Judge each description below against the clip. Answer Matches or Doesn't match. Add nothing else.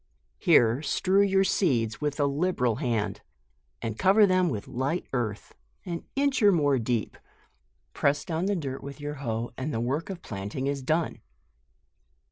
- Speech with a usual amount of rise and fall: Doesn't match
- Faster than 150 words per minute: Matches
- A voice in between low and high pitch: Matches